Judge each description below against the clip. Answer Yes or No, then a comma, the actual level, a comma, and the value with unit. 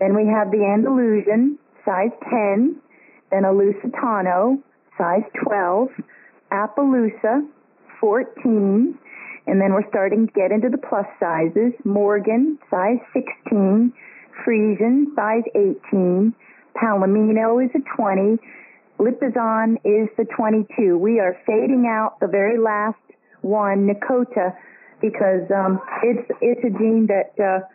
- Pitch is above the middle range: Yes, high, 220 Hz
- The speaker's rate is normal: No, slow, 120 wpm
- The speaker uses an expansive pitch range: No, average, 3.4 semitones